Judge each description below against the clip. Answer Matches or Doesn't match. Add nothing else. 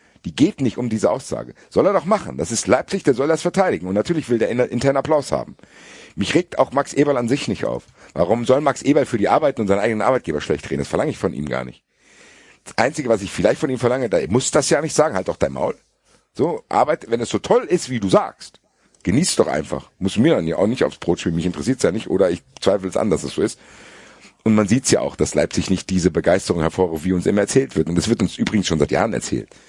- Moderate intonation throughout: Doesn't match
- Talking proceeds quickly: Matches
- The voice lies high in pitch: Doesn't match